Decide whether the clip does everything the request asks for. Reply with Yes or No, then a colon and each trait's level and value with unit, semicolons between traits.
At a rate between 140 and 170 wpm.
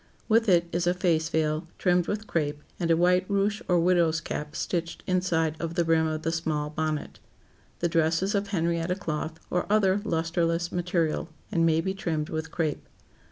No: average, 185 wpm